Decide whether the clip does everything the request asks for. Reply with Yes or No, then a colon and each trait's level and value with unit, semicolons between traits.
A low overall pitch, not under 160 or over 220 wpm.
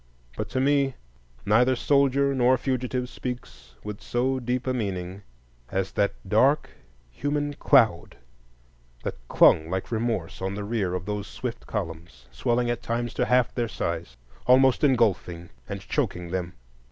No: low, 120 Hz; average, 145 wpm